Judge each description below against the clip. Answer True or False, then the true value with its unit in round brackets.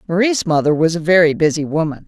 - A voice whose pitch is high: False (165 Hz)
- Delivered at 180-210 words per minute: True (205 wpm)